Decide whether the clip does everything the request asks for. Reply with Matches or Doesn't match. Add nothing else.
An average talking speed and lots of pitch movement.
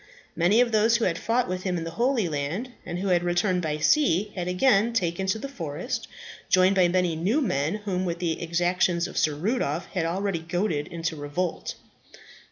Doesn't match